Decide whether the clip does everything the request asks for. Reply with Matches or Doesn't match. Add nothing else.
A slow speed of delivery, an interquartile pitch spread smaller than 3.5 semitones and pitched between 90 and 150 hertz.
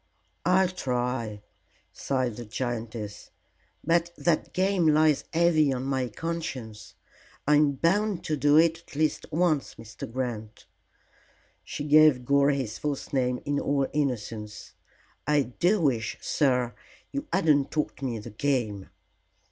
Doesn't match